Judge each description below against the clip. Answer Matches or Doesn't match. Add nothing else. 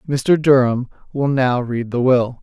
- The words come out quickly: Doesn't match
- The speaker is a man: Matches